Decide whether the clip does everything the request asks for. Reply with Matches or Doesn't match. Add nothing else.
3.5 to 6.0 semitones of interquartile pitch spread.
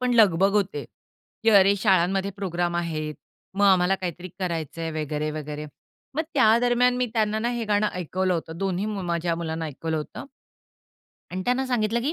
Matches